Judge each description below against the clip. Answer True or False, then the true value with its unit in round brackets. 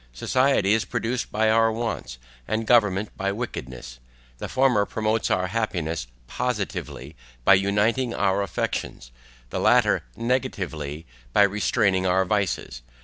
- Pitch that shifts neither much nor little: True (3.6 semitones)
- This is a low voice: True (100 Hz)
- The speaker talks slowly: True (125 wpm)